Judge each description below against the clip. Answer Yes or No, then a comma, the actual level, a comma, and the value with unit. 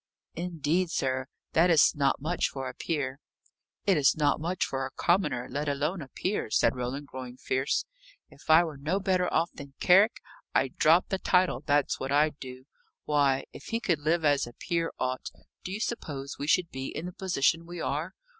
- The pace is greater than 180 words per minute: Yes, average, 190 wpm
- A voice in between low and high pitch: Yes, medium, 150 Hz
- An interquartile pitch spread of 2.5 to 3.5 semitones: No, average, 4.4 semitones